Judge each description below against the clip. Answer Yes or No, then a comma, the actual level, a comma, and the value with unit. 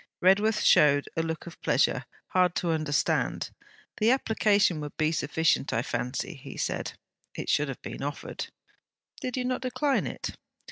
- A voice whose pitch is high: No, medium, 165 Hz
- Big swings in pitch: Yes, wide, 6.6 semitones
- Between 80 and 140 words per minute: No, average, 155 wpm